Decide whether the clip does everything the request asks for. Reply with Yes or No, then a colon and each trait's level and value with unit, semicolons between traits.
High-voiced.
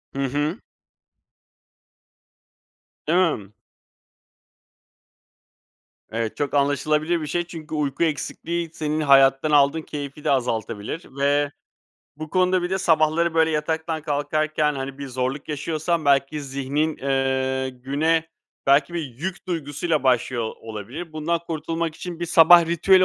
No: medium, 150 Hz